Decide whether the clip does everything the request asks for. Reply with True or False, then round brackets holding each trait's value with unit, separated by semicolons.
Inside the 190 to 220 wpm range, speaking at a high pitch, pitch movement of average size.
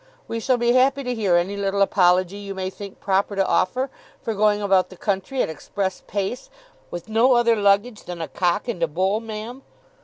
True (205 wpm; 200 Hz; 3.4 semitones)